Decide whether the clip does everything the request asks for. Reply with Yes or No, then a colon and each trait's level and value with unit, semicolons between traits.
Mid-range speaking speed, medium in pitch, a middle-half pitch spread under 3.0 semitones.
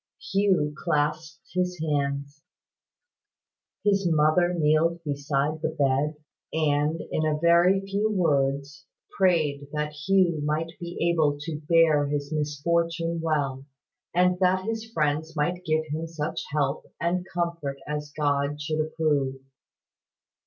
No: slow, 125 wpm; medium, 155 Hz; narrow, 2.6 semitones